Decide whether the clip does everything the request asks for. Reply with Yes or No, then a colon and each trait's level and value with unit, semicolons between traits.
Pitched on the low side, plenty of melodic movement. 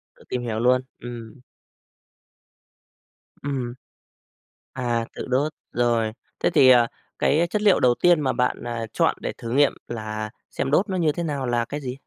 No: low, 125 Hz; average, 3.5 semitones